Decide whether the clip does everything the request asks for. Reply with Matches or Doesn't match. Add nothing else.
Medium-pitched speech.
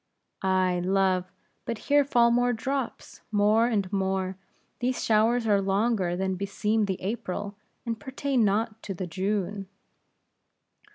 Doesn't match